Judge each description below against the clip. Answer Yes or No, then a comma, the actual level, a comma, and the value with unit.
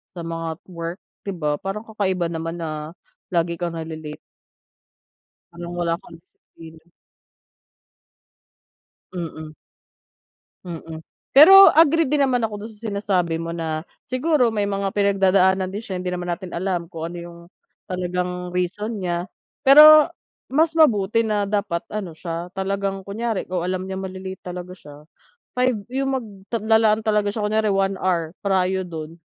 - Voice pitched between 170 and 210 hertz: Yes, high, 190 Hz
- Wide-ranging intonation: No, average, 3.8 semitones